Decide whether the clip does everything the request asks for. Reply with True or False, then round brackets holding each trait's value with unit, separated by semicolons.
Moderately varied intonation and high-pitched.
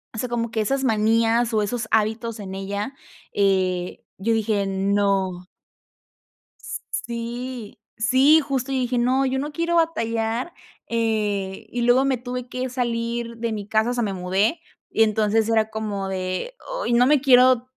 True (3.3 semitones; 230 Hz)